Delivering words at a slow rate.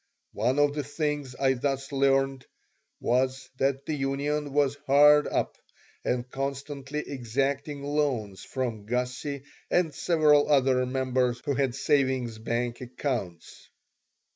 Yes: slow, 120 wpm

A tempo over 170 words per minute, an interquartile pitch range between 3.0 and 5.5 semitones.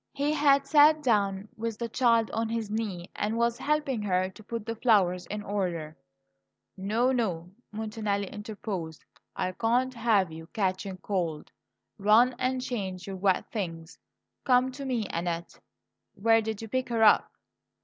No: average, 155 wpm; average, 4.0 semitones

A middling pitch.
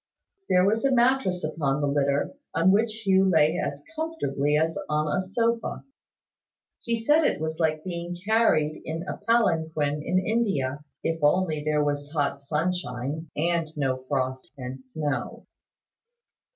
Yes: medium, 160 Hz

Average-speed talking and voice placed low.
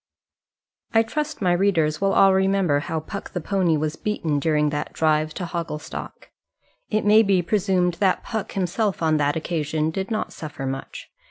No: average, 170 wpm; medium, 175 Hz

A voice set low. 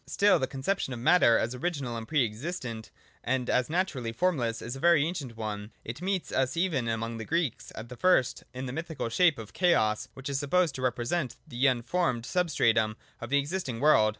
Yes: low, 130 Hz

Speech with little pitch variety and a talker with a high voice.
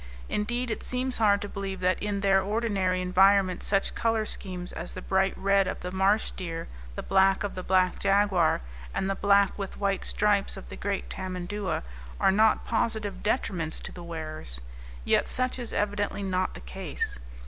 Yes: narrow, 2.0 semitones; high, 195 Hz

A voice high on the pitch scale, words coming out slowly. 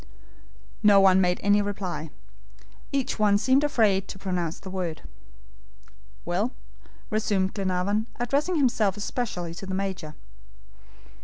Yes: high, 195 Hz; slow, 120 wpm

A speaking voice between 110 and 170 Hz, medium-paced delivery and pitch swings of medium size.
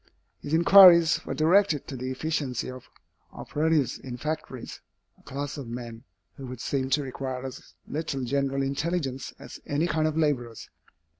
Yes: medium, 140 Hz; average, 155 wpm; average, 3.5 semitones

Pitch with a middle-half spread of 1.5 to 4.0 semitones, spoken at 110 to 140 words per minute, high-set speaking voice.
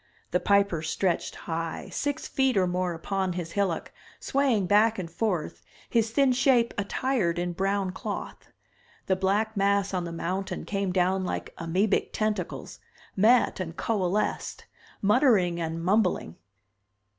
Yes: average, 3.5 semitones; slow, 135 wpm; high, 195 Hz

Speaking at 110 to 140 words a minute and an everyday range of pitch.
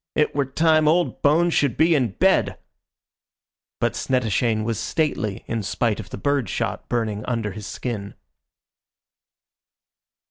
No: slow, 135 wpm; wide, 5.7 semitones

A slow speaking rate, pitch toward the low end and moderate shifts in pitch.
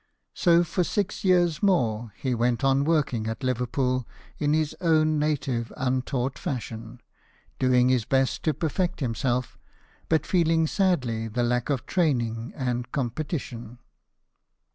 Yes: slow, 130 wpm; low, 130 Hz; average, 4.5 semitones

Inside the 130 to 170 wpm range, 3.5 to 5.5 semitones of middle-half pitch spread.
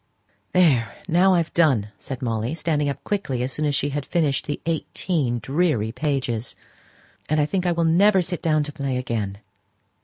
No: average, 180 wpm; average, 4.8 semitones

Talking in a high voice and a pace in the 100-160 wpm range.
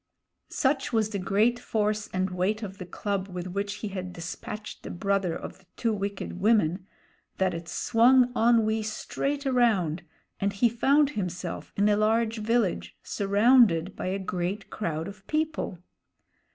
Yes: high, 205 Hz; average, 155 wpm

